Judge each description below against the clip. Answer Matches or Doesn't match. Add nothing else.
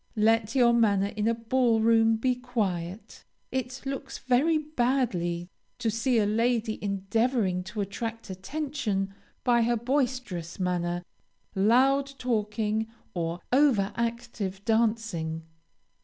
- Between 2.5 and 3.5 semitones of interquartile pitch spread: Doesn't match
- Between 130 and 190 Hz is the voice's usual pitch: Doesn't match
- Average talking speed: Doesn't match